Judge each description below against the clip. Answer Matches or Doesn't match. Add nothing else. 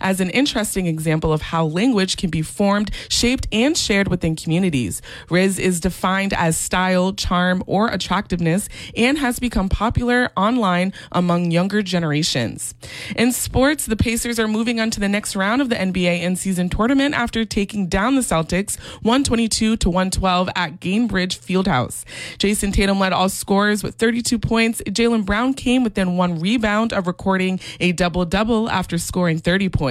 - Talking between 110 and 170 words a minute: Matches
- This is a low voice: Doesn't match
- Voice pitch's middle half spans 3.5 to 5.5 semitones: Matches